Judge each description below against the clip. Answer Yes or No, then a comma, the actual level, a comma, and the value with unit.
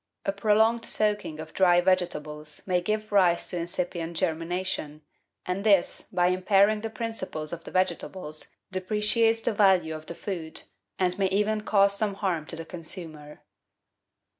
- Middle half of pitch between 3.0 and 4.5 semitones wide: Yes, average, 3.7 semitones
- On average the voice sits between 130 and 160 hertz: No, medium, 185 Hz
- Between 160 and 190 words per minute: No, average, 150 wpm